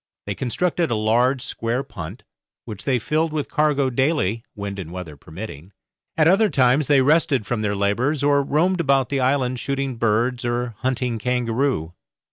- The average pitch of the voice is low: Yes, low, 125 Hz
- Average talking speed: Yes, average, 165 wpm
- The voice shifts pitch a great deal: No, average, 4.5 semitones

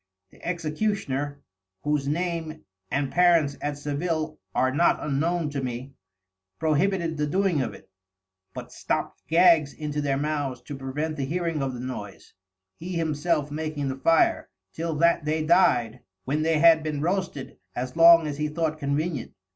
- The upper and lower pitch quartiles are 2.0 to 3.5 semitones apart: Yes, average, 2.9 semitones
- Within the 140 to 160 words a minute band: Yes, average, 155 wpm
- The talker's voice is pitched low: No, medium, 155 Hz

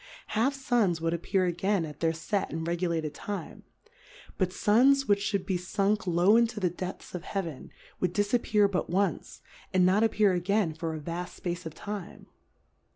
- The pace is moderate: Yes, average, 170 wpm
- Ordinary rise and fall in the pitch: Yes, average, 3.4 semitones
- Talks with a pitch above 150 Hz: Yes, medium, 185 Hz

